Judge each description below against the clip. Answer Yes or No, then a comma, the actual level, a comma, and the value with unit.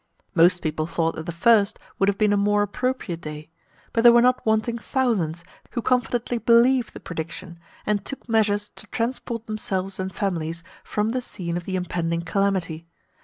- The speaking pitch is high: Yes, high, 200 Hz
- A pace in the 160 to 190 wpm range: Yes, average, 175 wpm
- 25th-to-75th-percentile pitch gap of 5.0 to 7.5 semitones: Yes, average, 5.3 semitones